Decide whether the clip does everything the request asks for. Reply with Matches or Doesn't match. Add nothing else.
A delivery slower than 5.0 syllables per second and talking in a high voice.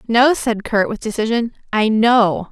Matches